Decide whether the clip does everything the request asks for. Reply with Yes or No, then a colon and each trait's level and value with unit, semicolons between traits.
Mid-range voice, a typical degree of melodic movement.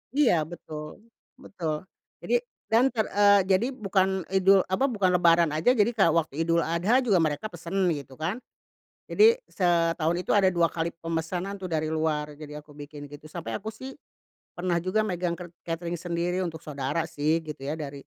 Yes: medium, 170 Hz; average, 3.5 semitones